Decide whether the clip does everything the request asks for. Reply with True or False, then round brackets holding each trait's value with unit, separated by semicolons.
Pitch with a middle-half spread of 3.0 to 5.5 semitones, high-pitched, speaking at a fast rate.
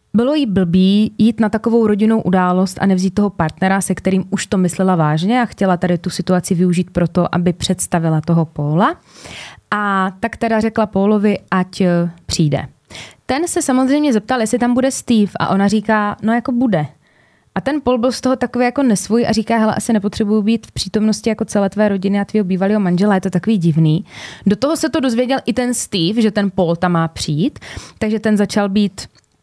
True (3.7 semitones; 205 Hz; 200 wpm)